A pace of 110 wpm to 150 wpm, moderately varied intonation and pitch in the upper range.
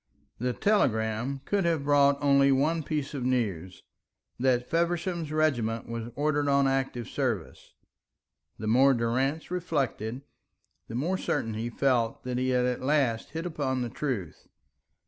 No: average, 145 wpm; average, 4.1 semitones; low, 135 Hz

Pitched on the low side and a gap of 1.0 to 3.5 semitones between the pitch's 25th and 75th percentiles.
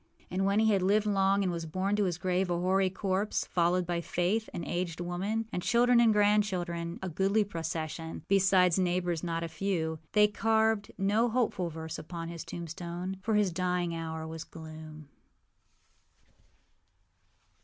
No: medium, 180 Hz; average, 3.0 semitones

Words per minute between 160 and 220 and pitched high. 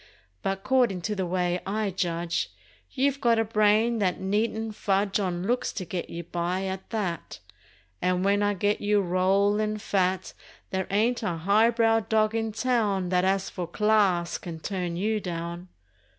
Yes: average, 165 wpm; high, 195 Hz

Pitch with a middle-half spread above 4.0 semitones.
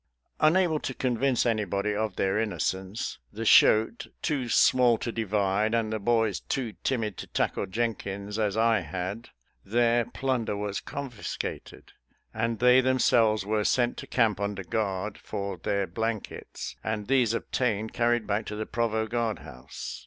No: average, 2.7 semitones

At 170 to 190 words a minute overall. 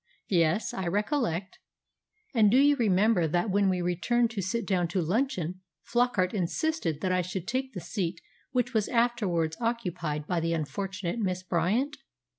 No: average, 160 wpm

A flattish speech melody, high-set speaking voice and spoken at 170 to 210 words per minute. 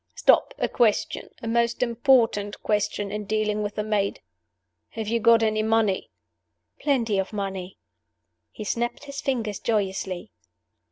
No: narrow, 2.3 semitones; high, 215 Hz; slow, 135 wpm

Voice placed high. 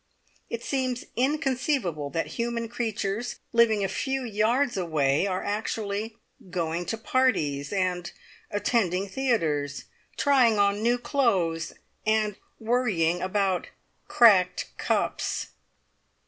Yes: high, 210 Hz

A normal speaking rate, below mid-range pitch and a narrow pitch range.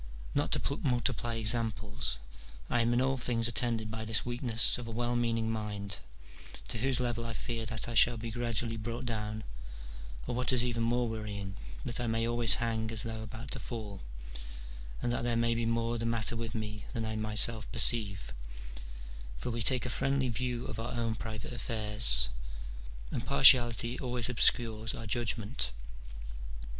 Yes: average, 170 wpm; low, 115 Hz; narrow, 1.5 semitones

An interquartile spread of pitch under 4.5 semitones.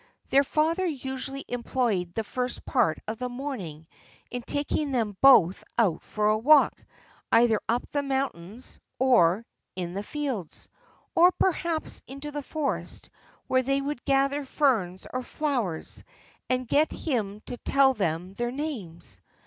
No: average, 5.0 semitones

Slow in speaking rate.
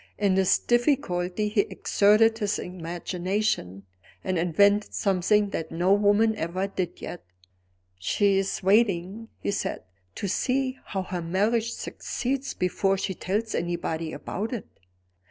Yes: slow, 125 wpm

